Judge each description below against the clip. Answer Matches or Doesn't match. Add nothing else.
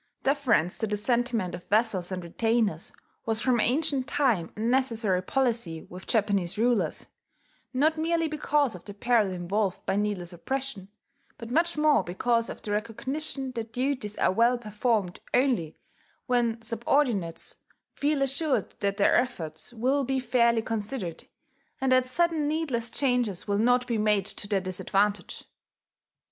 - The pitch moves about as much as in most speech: Matches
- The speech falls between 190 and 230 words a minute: Doesn't match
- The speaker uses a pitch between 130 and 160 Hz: Doesn't match